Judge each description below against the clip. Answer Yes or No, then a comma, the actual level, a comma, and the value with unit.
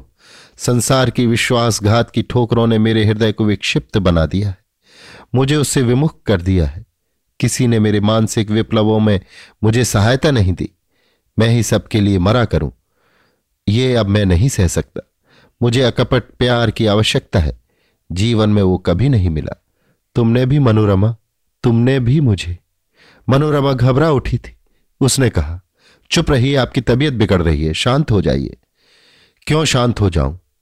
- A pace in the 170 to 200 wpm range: No, average, 155 wpm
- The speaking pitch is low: Yes, low, 110 Hz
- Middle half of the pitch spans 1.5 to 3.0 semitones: No, average, 4.4 semitones